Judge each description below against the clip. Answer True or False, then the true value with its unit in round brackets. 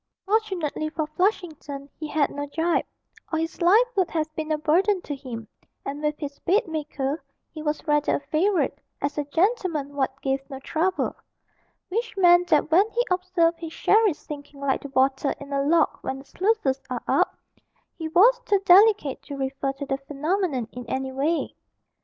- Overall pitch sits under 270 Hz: False (310 Hz)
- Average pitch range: True (4.4 semitones)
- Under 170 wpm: False (175 wpm)